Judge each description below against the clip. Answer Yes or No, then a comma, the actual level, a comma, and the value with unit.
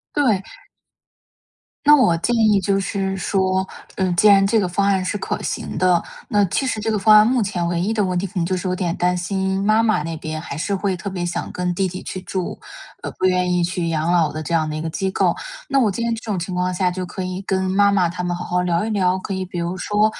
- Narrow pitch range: Yes, narrow, 2.3 semitones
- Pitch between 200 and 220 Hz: No, medium, 185 Hz